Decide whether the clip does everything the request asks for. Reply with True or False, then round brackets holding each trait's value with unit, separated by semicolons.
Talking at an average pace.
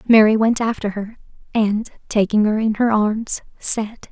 True (160 wpm)